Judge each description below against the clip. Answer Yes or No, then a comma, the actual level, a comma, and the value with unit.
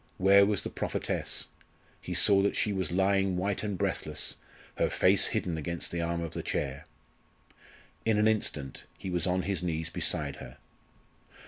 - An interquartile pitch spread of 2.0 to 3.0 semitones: Yes, average, 2.7 semitones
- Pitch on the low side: Yes, very low, 90 Hz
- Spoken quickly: No, average, 165 wpm